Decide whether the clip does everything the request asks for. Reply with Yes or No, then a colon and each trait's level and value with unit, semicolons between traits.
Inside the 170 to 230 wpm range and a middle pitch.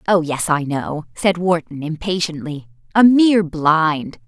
No: average, 140 wpm; medium, 165 Hz